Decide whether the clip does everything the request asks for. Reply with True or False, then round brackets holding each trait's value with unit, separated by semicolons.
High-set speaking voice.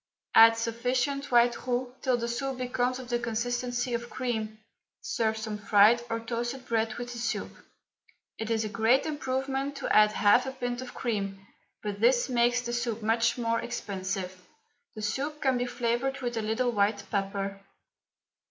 True (235 Hz)